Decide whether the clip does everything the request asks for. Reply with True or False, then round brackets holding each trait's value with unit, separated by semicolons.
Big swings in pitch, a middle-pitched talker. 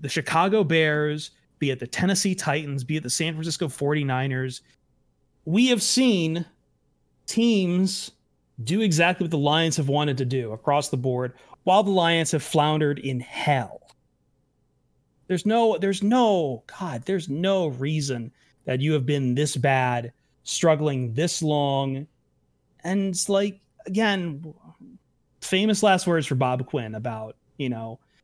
True (5.7 semitones; 150 Hz)